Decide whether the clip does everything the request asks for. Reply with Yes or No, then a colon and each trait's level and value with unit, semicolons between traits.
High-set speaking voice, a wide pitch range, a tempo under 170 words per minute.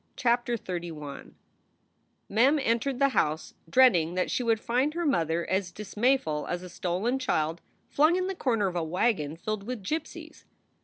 Yes: high, 215 Hz; wide, 6.9 semitones; average, 160 wpm